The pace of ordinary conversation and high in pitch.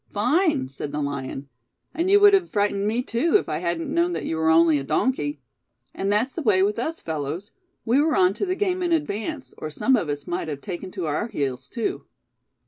No: fast, 225 wpm; high, 205 Hz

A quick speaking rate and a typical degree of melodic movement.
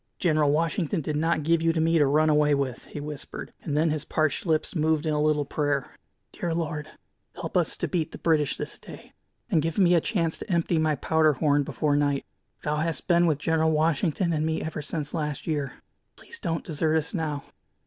No: fast, 210 wpm; narrow, 1.7 semitones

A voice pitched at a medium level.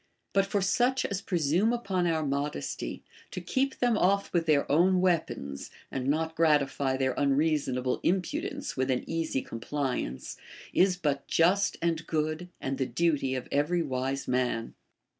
Yes: medium, 155 Hz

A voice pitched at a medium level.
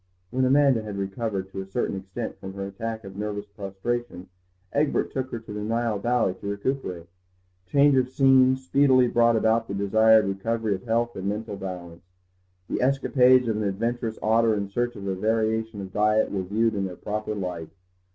No: low, 110 Hz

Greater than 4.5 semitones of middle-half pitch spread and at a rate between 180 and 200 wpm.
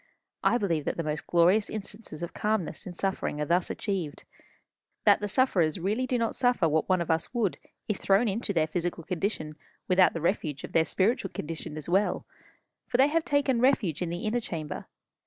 Yes: average, 4.9 semitones; average, 195 wpm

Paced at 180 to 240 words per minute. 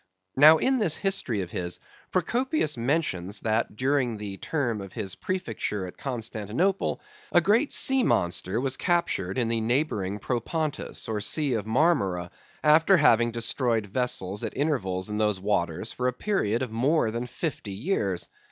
No: average, 155 wpm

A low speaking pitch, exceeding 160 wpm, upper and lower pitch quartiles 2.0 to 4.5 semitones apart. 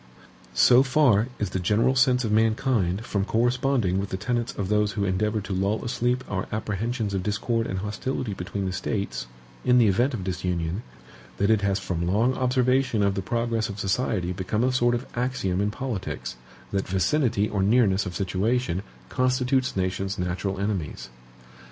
Yes: low, 105 Hz; average, 170 wpm; average, 4.2 semitones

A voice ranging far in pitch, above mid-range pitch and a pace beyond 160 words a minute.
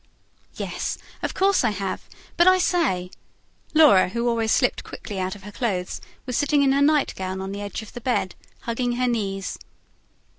Yes: wide, 6.0 semitones; high, 230 Hz; average, 180 wpm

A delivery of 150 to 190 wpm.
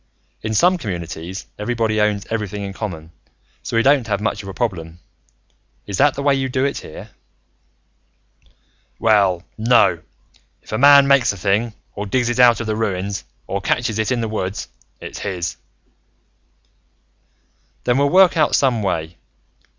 Yes: average, 165 wpm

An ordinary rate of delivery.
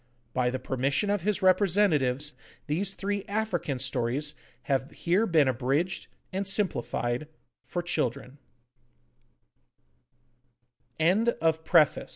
No: slow, 90 wpm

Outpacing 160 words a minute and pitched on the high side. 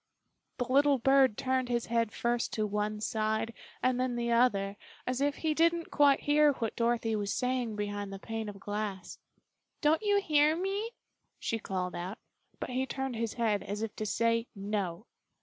Yes: average, 180 wpm; high, 235 Hz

